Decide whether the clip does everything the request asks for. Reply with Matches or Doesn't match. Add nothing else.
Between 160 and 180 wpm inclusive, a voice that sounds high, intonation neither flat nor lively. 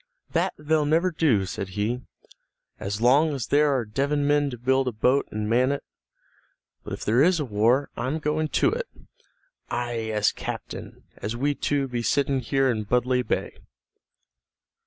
Doesn't match